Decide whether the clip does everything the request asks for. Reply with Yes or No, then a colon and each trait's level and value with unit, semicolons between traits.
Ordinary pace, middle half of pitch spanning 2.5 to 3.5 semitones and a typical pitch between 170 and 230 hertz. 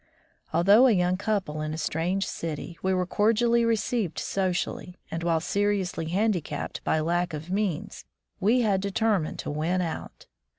No: average, 155 wpm; average, 3.9 semitones; medium, 185 Hz